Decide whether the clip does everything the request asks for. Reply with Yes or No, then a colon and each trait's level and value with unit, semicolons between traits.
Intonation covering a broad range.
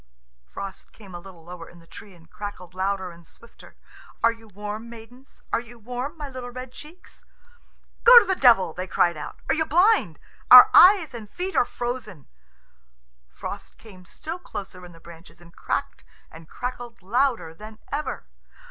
Yes: wide, 5.9 semitones